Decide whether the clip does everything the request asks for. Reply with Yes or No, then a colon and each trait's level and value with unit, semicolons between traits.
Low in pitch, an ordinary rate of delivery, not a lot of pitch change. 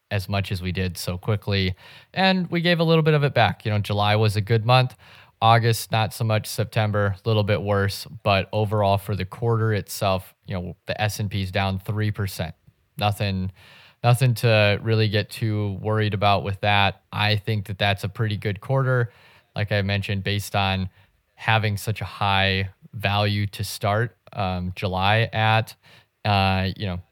Yes: low, 105 Hz; average, 185 wpm; narrow, 2.2 semitones